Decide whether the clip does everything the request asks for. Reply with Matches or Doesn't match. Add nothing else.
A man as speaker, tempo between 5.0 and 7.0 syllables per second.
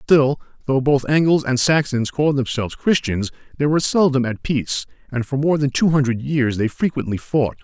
Matches